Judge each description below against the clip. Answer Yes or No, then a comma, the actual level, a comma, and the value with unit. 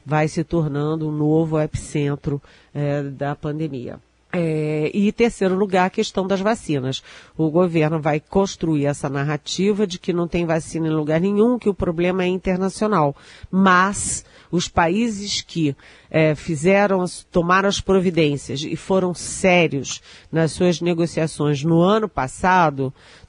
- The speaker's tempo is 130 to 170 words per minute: Yes, average, 140 wpm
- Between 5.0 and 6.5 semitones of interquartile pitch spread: No, average, 3.8 semitones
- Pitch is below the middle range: No, medium, 165 Hz